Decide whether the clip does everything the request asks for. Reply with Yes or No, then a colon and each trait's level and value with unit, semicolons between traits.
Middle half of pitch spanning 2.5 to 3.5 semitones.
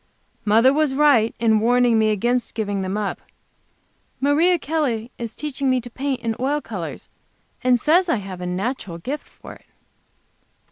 No: average, 4.6 semitones